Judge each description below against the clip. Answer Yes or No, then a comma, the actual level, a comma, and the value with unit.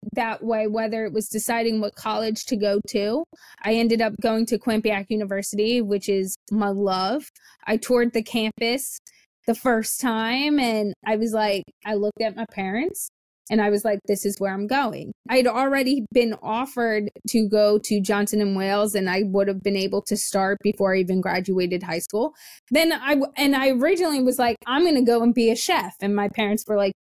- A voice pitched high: Yes, high, 220 Hz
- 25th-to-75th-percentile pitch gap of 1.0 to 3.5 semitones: Yes, average, 2.8 semitones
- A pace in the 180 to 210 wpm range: Yes, average, 200 wpm